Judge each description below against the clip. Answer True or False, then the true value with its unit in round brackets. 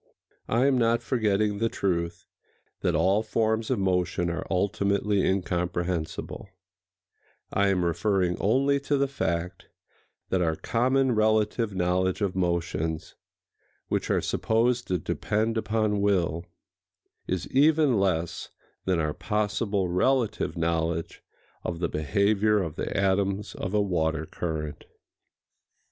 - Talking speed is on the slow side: True (125 wpm)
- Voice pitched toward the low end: True (100 Hz)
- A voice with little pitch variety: False (3.9 semitones)